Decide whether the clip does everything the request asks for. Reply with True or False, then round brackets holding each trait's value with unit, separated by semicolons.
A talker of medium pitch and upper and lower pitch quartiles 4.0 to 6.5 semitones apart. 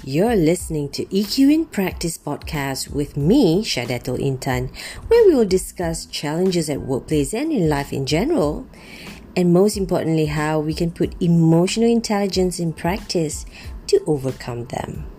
True (170 Hz; 5.1 semitones)